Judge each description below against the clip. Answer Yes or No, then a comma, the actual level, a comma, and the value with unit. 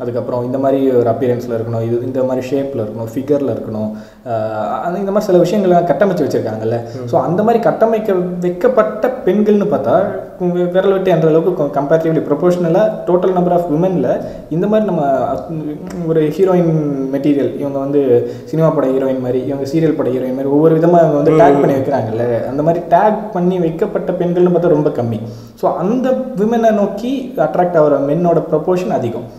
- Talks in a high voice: No, medium, 160 Hz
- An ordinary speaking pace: No, fast, 160 wpm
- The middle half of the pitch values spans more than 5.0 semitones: Yes, wide, 5.5 semitones